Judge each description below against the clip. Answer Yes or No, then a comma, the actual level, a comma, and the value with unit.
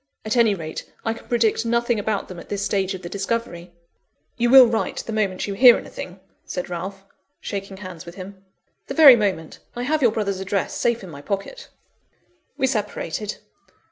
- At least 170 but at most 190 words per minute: Yes, average, 185 wpm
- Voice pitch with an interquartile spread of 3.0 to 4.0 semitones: Yes, average, 3.6 semitones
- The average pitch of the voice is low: No, high, 205 Hz